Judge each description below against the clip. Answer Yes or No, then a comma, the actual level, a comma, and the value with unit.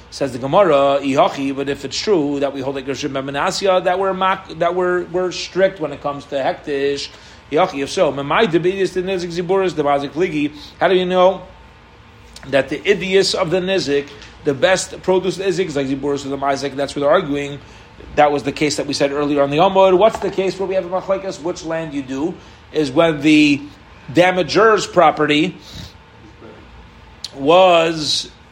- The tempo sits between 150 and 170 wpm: Yes, average, 155 wpm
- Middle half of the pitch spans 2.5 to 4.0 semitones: No, average, 4.7 semitones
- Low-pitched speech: No, medium, 150 Hz